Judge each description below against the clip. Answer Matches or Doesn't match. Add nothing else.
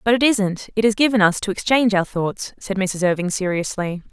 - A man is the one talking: Doesn't match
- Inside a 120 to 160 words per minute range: Doesn't match